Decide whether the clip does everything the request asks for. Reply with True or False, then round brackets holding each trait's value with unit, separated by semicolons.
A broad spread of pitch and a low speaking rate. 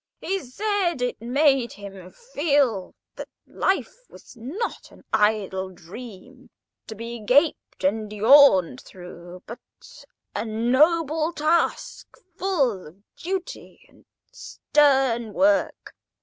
True (6.9 semitones; 105 wpm)